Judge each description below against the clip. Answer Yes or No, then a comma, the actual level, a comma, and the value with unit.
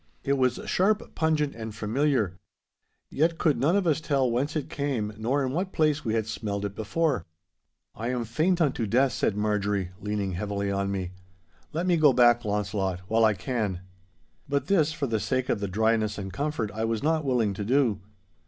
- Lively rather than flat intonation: Yes, wide, 5.8 semitones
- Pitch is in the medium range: No, low, 115 Hz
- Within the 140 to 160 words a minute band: No, average, 190 wpm